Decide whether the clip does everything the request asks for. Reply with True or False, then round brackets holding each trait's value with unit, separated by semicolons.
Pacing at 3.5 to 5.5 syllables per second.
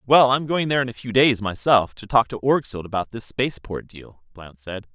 True (5.3 syllables/s)